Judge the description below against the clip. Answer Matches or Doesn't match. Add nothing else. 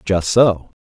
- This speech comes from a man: Matches